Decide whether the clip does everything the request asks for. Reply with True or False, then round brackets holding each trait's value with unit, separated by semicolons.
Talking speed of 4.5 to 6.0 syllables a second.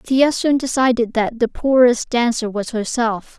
False (4.3 syllables/s)